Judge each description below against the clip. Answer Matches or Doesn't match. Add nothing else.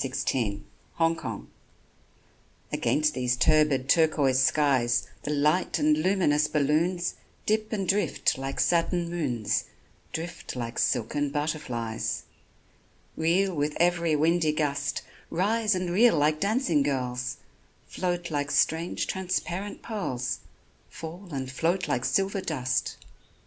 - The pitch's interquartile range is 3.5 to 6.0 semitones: Matches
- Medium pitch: Matches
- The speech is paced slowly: Matches